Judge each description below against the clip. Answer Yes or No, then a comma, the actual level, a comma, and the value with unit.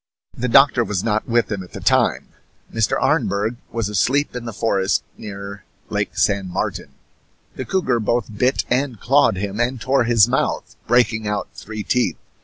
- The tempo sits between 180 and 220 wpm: No, average, 170 wpm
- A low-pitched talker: Yes, low, 115 Hz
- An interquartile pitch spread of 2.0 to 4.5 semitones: Yes, average, 3.2 semitones